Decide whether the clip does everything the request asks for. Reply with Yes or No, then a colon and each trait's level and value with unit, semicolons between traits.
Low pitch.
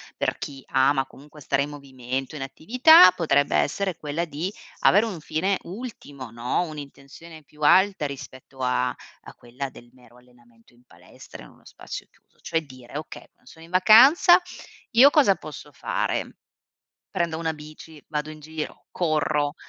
No: medium, 150 Hz